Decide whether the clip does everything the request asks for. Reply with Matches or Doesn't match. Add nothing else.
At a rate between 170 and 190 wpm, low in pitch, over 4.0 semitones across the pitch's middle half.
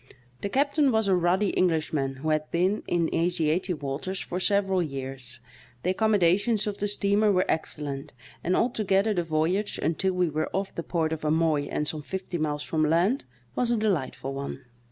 Doesn't match